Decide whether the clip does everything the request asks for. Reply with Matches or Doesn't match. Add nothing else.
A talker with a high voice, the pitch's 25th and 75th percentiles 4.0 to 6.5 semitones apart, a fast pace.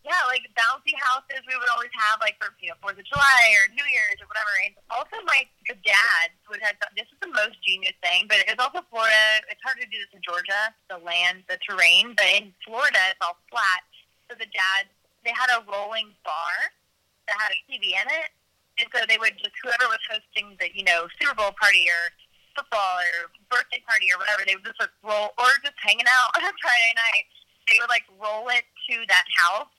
Matches